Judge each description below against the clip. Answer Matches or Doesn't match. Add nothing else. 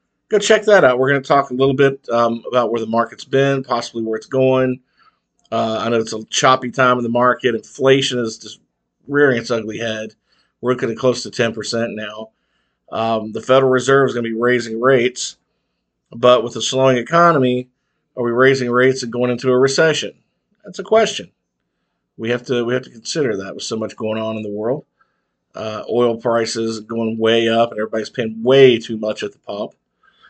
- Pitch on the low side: Matches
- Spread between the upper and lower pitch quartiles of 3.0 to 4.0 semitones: Doesn't match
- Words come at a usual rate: Doesn't match